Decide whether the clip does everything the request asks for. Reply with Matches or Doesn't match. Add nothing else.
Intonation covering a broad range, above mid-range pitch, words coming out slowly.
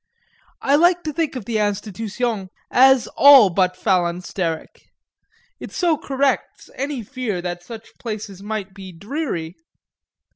Matches